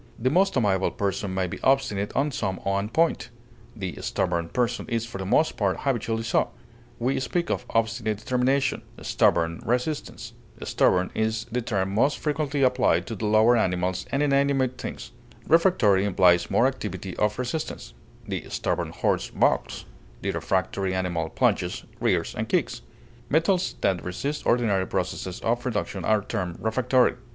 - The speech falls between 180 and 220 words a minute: No, average, 150 wpm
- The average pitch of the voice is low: Yes, low, 115 Hz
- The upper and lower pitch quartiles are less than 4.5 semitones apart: No, average, 5.3 semitones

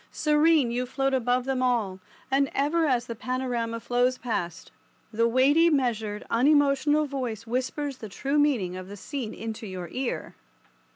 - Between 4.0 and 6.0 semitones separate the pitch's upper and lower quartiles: No, average, 3.5 semitones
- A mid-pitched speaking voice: No, very high, 250 Hz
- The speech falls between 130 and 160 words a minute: Yes, average, 155 wpm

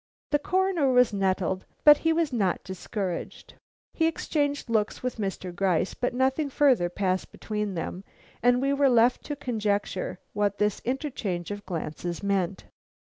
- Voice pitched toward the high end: Yes, high, 210 Hz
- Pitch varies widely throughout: Yes, wide, 6.3 semitones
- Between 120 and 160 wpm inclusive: Yes, average, 150 wpm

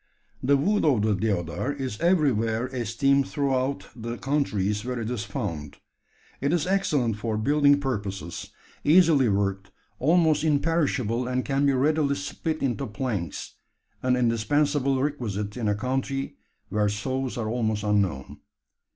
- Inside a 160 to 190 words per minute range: No, slow, 135 wpm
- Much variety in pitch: No, average, 5.0 semitones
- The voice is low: Yes, low, 125 Hz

